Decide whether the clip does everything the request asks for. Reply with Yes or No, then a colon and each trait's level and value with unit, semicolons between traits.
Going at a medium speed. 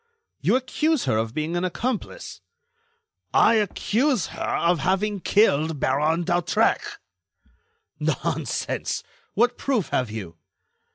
No: slow, 110 wpm